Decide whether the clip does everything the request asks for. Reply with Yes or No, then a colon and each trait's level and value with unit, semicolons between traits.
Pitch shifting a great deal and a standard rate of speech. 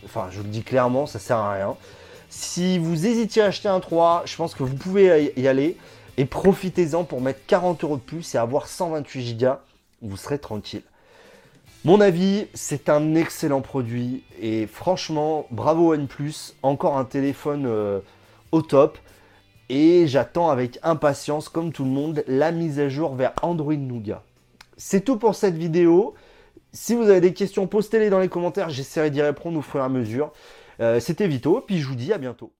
Yes: wide, 5.8 semitones; average, 185 wpm